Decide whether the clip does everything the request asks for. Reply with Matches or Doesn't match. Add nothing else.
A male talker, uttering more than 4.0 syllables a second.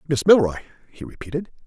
Matches